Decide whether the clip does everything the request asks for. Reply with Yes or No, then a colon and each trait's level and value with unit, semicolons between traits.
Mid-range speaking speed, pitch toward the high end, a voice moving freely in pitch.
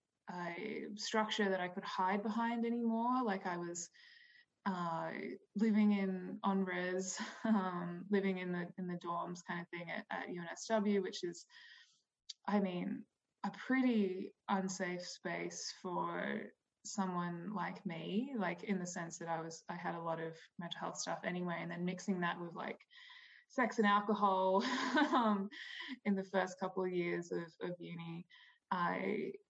No: average, 155 wpm; high, 195 Hz; average, 3.9 semitones